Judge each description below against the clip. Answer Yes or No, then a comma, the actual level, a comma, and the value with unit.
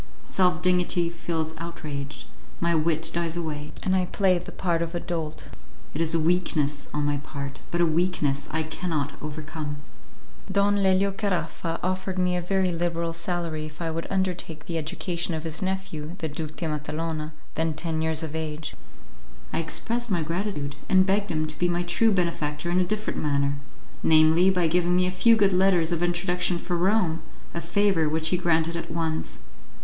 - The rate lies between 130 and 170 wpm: No, average, 185 wpm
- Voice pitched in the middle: Yes, medium, 170 Hz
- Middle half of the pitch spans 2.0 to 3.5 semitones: Yes, narrow, 2.4 semitones